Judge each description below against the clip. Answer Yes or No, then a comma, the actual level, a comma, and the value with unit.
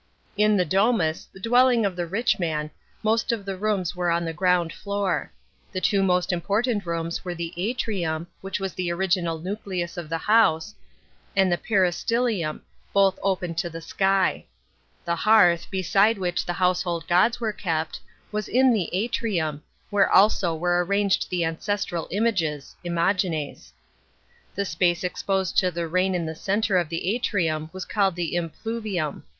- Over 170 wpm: No, average, 165 wpm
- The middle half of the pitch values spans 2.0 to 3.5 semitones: Yes, average, 3.2 semitones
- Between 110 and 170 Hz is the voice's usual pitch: No, medium, 185 Hz